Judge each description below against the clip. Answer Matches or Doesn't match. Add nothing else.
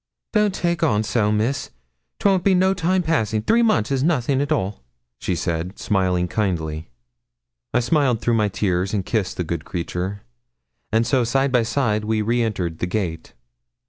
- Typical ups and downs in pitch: Doesn't match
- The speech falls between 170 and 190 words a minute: Matches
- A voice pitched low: Matches